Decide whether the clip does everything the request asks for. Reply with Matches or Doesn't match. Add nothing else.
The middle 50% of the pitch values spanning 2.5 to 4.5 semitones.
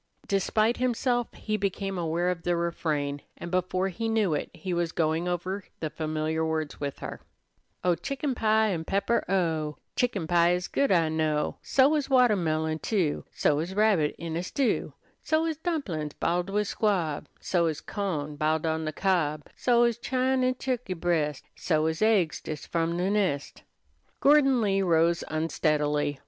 Doesn't match